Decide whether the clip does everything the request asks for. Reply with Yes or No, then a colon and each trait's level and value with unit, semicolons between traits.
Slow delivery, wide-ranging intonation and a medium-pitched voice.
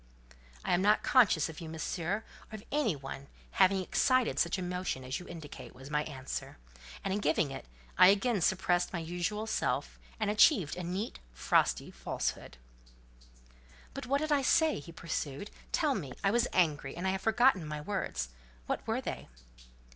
No: average, 170 wpm; wide, 5.9 semitones; medium, 180 Hz